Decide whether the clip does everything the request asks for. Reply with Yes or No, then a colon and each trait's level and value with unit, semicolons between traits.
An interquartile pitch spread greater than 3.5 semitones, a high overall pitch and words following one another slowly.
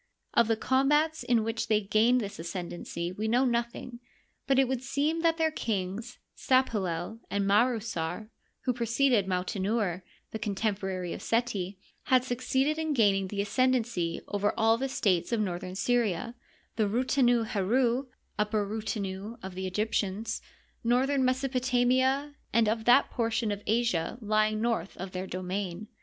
No: average, 4.1 semitones; high, 225 Hz; average, 150 wpm